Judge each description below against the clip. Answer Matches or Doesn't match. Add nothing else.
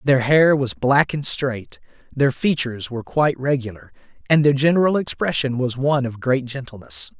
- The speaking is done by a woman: Doesn't match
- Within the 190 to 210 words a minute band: Doesn't match